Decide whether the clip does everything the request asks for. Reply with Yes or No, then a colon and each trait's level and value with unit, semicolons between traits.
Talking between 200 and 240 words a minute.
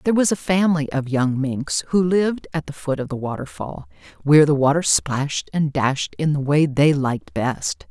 Yes: fast, 205 wpm